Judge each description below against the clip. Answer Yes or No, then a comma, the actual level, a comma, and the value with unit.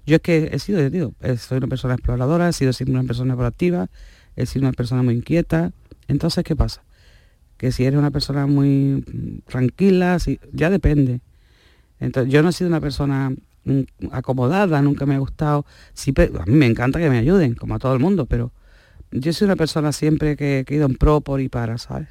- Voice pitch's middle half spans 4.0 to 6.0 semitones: No, average, 3.6 semitones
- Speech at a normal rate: No, fast, 205 wpm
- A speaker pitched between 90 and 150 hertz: Yes, low, 135 Hz